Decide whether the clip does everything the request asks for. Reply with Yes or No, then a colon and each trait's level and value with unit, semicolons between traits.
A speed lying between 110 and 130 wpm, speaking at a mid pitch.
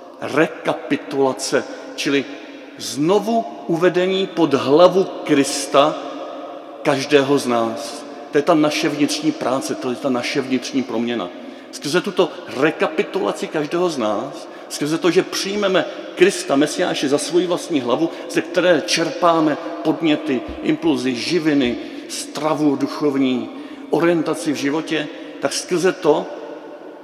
Yes: slow, 115 wpm; medium, 165 Hz